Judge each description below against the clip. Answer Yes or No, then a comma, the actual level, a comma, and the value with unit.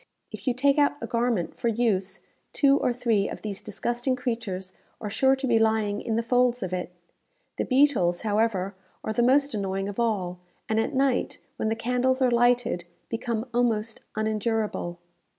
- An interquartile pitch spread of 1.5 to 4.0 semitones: Yes, average, 3.2 semitones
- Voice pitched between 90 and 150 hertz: No, high, 230 Hz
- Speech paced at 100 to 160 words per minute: No, average, 175 wpm